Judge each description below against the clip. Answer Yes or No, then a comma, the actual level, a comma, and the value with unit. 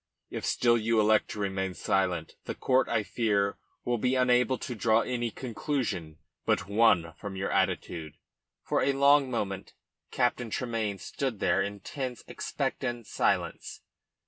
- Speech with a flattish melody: No, average, 3.9 semitones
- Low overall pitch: Yes, low, 115 Hz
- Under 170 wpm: Yes, average, 145 wpm